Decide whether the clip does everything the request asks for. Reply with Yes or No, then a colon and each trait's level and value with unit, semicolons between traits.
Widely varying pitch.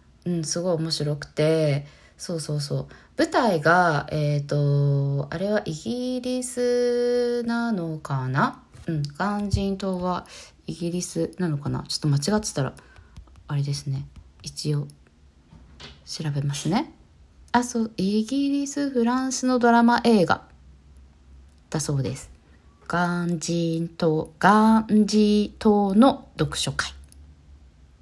Yes: wide, 7.3 semitones